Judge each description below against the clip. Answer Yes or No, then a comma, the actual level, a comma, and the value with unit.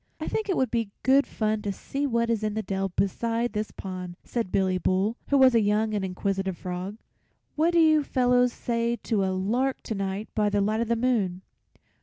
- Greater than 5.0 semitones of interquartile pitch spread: No, average, 3.9 semitones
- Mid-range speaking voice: No, high, 215 Hz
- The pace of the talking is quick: Yes, fast, 215 wpm